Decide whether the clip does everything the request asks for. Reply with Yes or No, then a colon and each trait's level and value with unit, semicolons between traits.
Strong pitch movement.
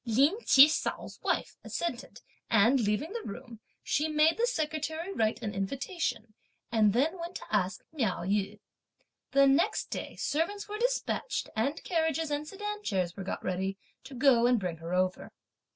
Yes: wide, 7.5 semitones